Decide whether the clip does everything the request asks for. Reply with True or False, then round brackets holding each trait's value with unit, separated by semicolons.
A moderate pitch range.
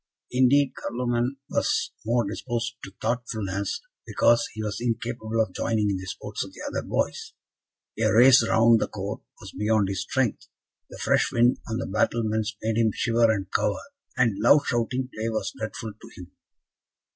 False (2.1 semitones)